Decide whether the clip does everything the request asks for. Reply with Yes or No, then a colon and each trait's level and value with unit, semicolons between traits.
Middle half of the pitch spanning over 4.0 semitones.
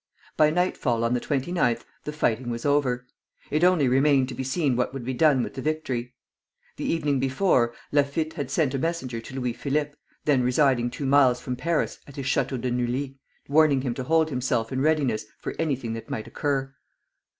No: average, 3.2 semitones